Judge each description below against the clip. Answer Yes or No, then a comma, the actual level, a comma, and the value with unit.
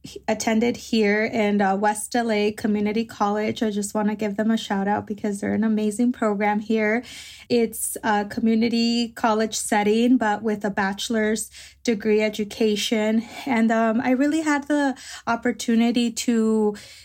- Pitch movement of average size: No, narrow, 1.8 semitones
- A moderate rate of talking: Yes, average, 150 wpm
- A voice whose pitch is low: No, high, 220 Hz